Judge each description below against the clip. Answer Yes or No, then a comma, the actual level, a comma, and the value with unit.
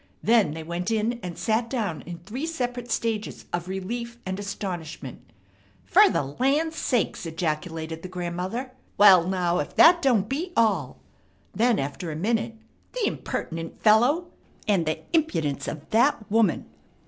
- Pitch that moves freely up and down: Yes, wide, 5.8 semitones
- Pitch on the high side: Yes, high, 205 Hz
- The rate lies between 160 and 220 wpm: No, average, 150 wpm